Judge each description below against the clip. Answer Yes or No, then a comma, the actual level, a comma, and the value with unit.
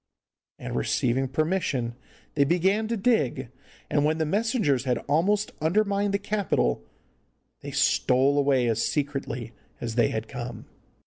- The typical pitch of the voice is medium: Yes, medium, 145 Hz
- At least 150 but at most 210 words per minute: No, slow, 135 wpm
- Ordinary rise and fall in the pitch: No, wide, 8.1 semitones